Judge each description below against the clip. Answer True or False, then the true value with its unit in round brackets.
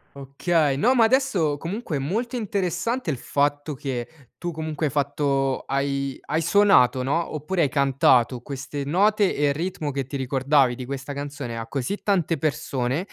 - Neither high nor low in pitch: True (145 Hz)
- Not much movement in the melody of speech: False (4.2 semitones)